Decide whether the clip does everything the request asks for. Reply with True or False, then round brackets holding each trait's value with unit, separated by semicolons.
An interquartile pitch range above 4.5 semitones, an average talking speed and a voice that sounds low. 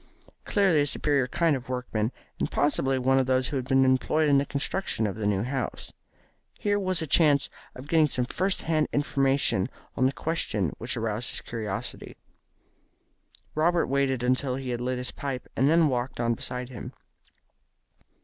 False (2.9 semitones; 180 wpm; 130 Hz)